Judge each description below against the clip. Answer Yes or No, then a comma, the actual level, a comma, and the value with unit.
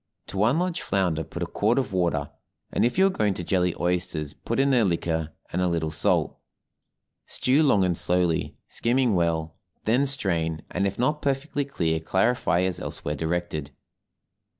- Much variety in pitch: Yes, wide, 7.1 semitones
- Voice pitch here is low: Yes, very low, 95 Hz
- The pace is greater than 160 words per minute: Yes, average, 175 wpm